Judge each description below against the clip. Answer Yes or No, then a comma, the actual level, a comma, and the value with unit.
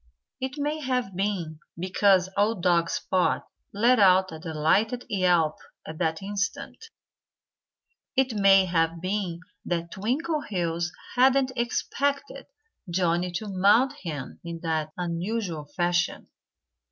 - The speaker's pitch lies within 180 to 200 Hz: Yes, medium, 185 Hz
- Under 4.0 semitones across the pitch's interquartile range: No, average, 5.0 semitones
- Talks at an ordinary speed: No, slow, 115 wpm